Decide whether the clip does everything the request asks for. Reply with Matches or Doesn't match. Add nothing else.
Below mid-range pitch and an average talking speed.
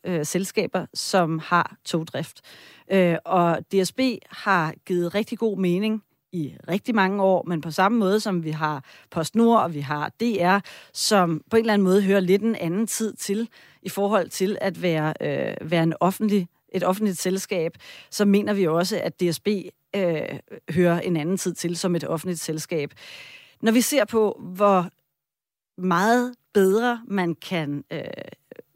Doesn't match